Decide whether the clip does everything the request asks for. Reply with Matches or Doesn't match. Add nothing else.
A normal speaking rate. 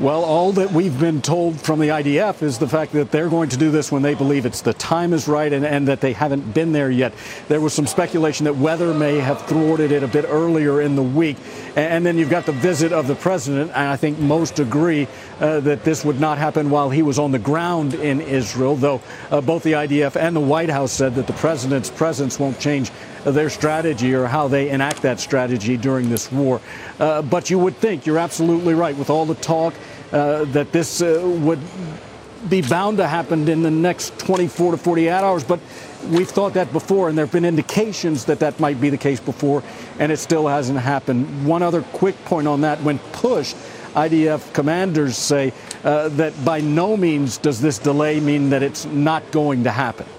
Doesn't match